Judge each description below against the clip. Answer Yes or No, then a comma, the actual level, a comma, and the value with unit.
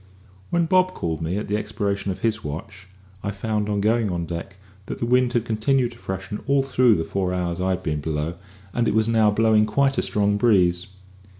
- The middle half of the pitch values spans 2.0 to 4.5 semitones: Yes, average, 3.9 semitones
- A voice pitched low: Yes, low, 105 Hz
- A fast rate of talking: Yes, fast, 215 wpm